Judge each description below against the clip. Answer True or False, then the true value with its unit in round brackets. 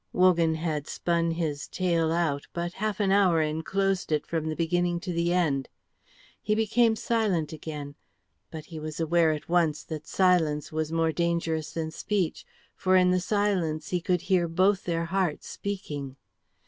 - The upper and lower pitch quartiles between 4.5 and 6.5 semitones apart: False (2.7 semitones)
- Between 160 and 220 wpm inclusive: True (165 wpm)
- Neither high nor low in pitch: True (170 Hz)